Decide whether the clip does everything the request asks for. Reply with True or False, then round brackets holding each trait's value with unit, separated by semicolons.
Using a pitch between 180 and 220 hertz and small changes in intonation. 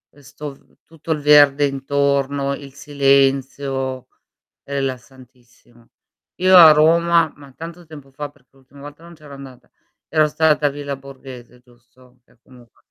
False (140 Hz; 2.0 semitones)